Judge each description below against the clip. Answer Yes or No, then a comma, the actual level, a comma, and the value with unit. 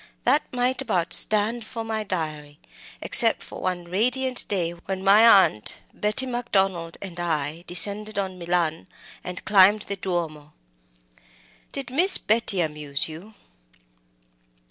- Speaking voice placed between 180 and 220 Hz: Yes, high, 190 Hz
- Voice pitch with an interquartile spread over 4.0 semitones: Yes, average, 4.5 semitones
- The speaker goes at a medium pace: No, slow, 125 wpm